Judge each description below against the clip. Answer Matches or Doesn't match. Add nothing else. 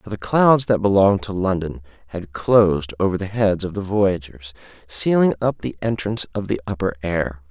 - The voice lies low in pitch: Matches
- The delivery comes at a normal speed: Matches